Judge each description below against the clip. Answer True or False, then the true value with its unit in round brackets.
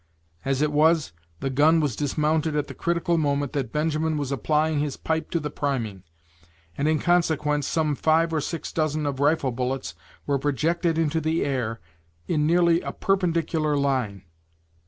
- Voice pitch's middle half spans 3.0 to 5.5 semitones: False (2.4 semitones)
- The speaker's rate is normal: True (165 wpm)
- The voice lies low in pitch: False (150 Hz)